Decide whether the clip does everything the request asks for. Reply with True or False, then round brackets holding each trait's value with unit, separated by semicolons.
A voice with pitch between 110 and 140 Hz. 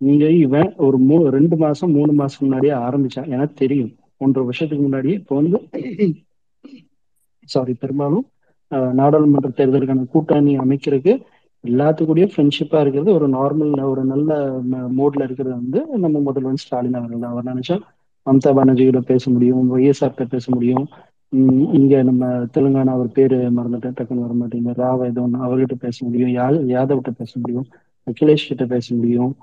True (135 Hz)